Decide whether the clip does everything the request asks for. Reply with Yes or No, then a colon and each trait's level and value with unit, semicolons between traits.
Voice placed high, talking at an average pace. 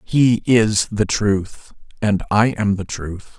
No: low, 105 Hz; average, 160 wpm